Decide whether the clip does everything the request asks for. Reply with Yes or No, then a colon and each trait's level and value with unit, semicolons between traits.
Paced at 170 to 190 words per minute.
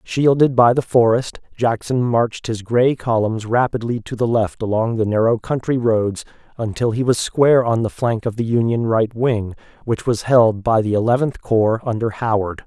Yes: average, 185 wpm